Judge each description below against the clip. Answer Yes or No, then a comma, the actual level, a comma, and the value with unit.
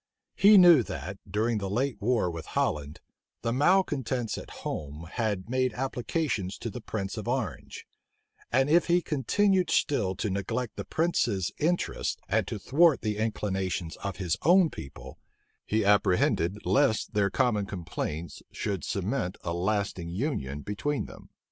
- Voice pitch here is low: Yes, low, 110 Hz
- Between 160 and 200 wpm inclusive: No, average, 150 wpm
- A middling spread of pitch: No, wide, 6.1 semitones